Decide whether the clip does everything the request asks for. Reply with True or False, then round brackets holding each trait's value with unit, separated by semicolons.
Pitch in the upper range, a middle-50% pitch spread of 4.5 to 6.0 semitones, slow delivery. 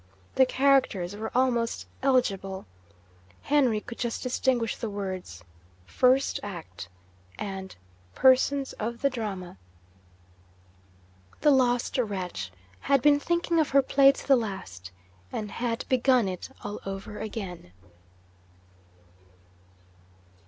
True (230 Hz; 5.3 semitones; 110 wpm)